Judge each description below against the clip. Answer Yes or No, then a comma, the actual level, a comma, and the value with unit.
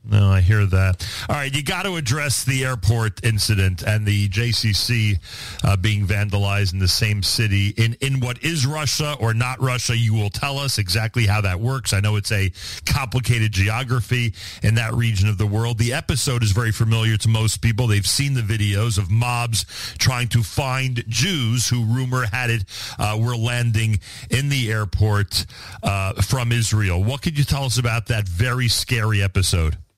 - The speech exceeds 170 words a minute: Yes, average, 185 wpm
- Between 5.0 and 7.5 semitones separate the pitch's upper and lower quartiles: No, average, 3.2 semitones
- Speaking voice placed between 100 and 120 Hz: Yes, low, 110 Hz